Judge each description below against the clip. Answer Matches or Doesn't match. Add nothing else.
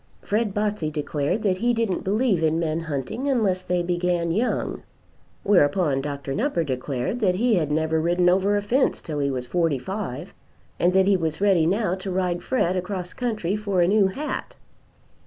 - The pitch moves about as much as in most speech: Matches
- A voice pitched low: Doesn't match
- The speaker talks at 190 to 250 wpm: Doesn't match